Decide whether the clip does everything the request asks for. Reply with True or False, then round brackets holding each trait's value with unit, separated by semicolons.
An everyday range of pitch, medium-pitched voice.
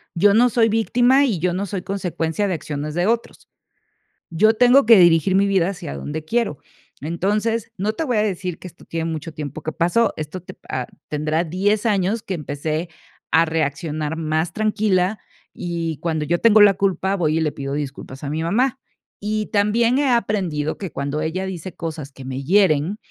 True (5.0 semitones; 180 Hz)